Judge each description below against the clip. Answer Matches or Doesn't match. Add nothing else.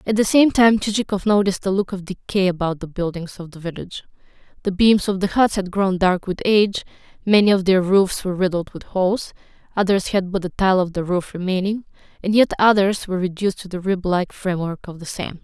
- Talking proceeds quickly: Matches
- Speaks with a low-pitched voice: Doesn't match